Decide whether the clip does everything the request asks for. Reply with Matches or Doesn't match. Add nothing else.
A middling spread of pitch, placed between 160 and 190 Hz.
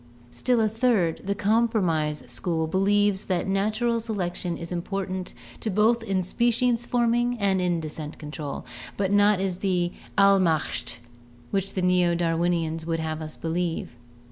Matches